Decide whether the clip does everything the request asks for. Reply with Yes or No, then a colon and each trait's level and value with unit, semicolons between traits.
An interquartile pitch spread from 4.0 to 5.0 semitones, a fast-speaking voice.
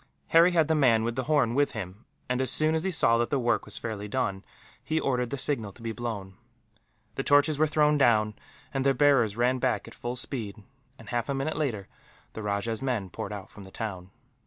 Yes: average, 4.7 semitones; fast, 225 wpm